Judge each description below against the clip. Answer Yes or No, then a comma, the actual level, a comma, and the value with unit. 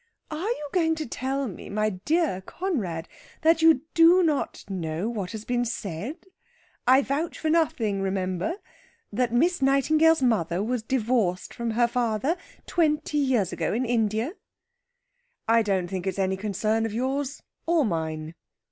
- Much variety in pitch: Yes, wide, 7.2 semitones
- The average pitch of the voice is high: Yes, high, 240 Hz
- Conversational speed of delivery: Yes, average, 155 wpm